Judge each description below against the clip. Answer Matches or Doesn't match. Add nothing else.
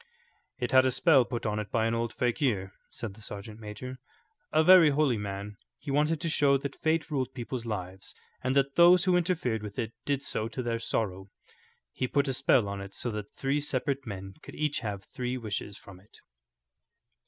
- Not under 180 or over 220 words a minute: Matches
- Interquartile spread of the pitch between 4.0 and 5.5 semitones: Matches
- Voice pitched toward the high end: Doesn't match